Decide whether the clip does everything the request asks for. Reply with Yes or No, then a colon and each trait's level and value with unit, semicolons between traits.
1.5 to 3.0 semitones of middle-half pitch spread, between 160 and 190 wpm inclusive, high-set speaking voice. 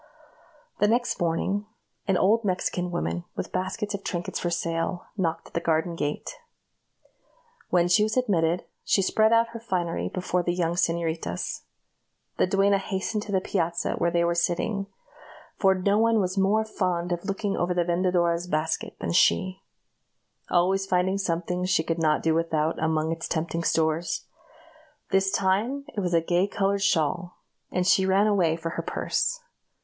No: average, 2.7 semitones; average, 165 wpm; medium, 180 Hz